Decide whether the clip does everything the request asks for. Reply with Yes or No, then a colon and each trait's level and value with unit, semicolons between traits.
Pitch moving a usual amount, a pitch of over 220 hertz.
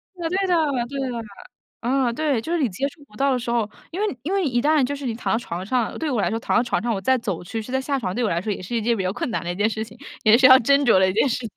Yes: average, 4.2 semitones; high, 240 Hz